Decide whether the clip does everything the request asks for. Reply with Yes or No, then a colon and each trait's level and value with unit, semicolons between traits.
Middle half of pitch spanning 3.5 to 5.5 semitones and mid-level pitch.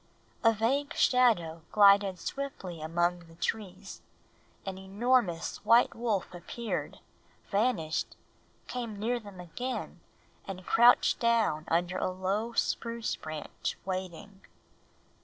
No: average, 4.8 semitones; high, 200 Hz